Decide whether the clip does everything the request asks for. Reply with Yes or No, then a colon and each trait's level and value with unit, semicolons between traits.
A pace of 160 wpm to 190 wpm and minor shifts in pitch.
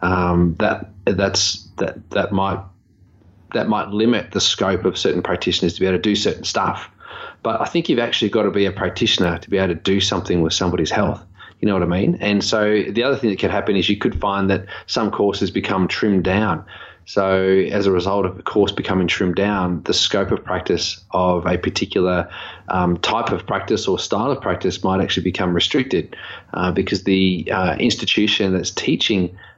No: average, 200 wpm; narrow, 1.8 semitones